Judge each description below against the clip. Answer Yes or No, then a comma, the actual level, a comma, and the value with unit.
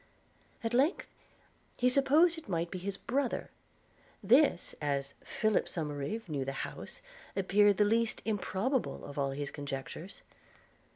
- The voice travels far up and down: Yes, wide, 8.8 semitones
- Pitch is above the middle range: Yes, high, 200 Hz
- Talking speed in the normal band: No, slow, 130 wpm